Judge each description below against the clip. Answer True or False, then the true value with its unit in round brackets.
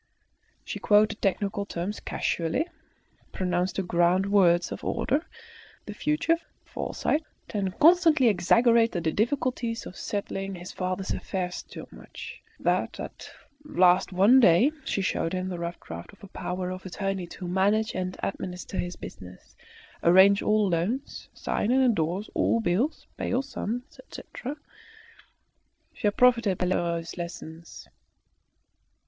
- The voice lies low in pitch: False (195 Hz)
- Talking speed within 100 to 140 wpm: True (135 wpm)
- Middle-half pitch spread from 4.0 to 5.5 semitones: True (4.4 semitones)